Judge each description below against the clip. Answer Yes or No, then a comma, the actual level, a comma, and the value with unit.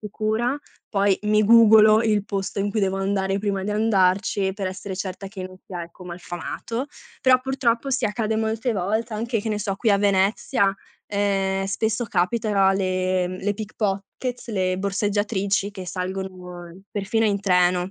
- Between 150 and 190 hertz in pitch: No, high, 200 Hz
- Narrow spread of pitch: Yes, narrow, 2.3 semitones